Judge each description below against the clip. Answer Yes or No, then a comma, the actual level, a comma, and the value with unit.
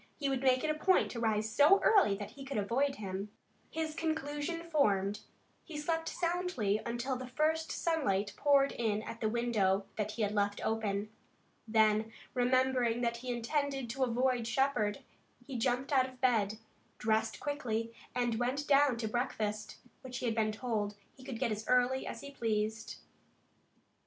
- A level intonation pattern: No, average, 4.3 semitones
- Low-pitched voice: No, high, 245 Hz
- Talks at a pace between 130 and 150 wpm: No, average, 170 wpm